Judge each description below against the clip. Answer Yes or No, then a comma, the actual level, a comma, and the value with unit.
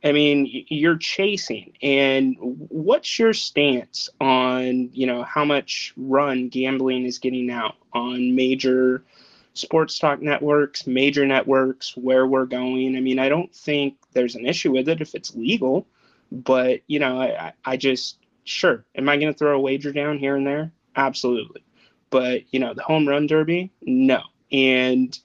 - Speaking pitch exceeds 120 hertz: Yes, low, 135 Hz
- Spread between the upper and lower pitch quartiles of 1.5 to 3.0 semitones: Yes, narrow, 2.4 semitones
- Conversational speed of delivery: Yes, average, 165 wpm